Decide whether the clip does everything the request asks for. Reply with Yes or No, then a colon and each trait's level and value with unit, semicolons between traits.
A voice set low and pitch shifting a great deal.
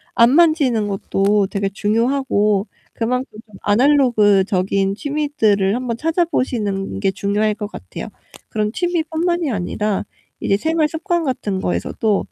No: high, 215 Hz; wide, 6.4 semitones